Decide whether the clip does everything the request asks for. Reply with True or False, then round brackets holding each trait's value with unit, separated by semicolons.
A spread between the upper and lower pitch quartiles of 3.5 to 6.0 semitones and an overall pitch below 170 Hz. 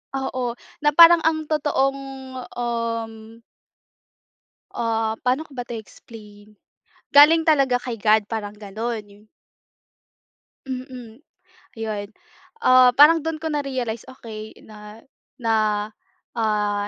False (3.9 semitones; 235 Hz)